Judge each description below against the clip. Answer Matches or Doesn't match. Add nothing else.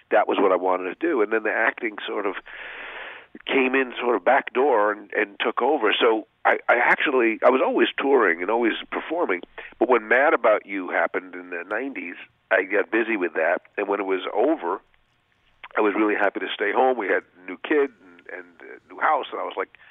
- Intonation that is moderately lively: Doesn't match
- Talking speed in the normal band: Doesn't match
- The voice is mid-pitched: Doesn't match